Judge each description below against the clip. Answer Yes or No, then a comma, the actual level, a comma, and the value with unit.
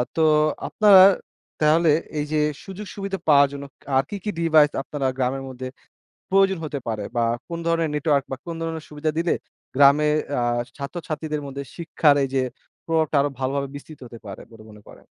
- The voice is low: No, medium, 150 Hz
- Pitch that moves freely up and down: No, average, 3.1 semitones